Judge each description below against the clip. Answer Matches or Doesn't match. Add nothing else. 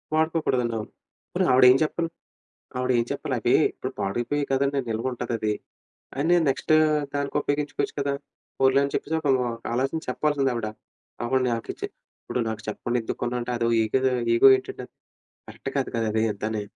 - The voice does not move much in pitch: Doesn't match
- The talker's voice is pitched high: Doesn't match